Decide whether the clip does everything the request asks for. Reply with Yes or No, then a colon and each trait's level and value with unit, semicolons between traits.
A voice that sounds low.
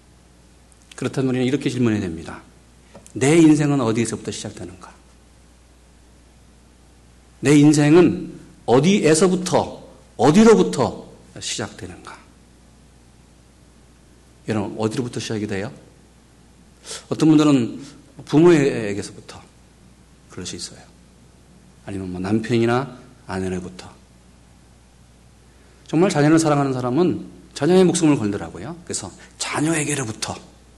Yes: very low, 95 Hz